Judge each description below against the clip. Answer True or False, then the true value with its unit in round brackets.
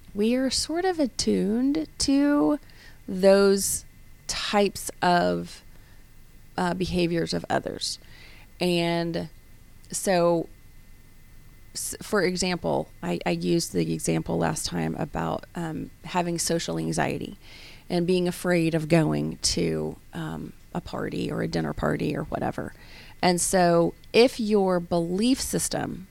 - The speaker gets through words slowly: True (115 wpm)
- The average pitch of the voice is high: False (170 Hz)